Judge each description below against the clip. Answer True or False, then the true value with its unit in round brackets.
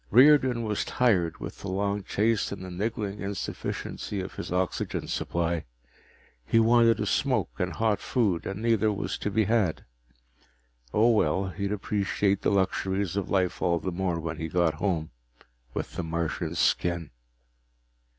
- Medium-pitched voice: False (95 Hz)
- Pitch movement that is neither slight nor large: True (3.6 semitones)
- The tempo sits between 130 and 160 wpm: True (155 wpm)